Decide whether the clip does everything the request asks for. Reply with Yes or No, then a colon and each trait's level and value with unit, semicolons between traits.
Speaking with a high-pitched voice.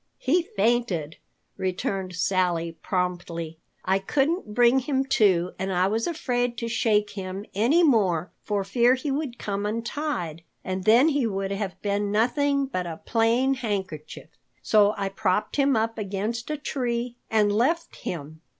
Yes: high, 210 Hz